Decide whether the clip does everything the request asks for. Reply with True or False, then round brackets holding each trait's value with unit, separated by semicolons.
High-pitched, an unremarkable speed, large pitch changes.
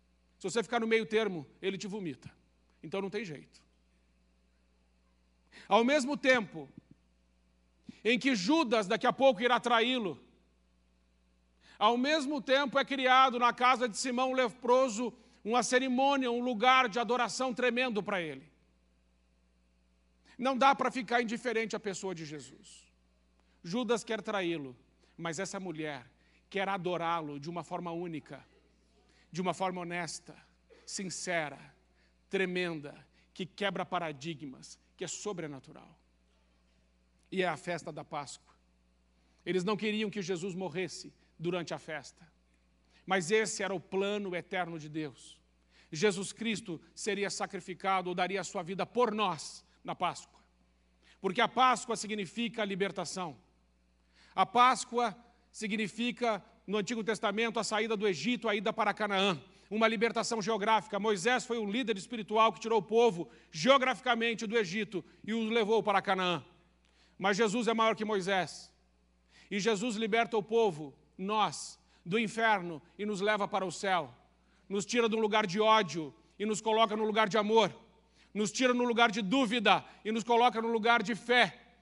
True (195 Hz; 145 wpm; 7.0 semitones)